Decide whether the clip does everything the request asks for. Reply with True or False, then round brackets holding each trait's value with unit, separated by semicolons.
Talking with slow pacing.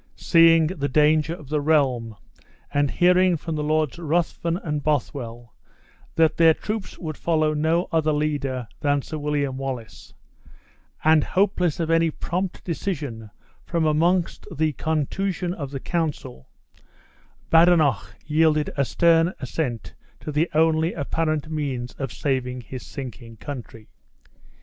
True (130 wpm)